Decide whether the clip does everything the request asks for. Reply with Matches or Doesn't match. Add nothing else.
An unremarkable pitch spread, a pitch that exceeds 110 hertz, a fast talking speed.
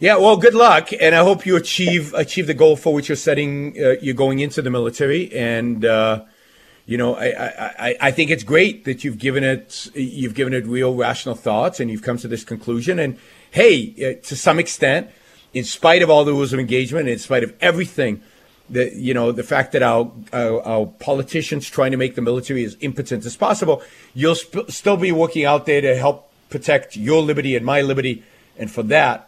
Matches